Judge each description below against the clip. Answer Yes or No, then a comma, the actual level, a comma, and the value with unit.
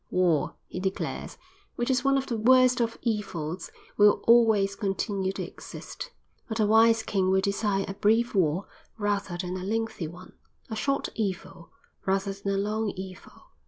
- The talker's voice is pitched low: No, high, 200 Hz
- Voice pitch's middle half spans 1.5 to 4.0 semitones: Yes, average, 3.0 semitones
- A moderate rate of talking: Yes, average, 165 wpm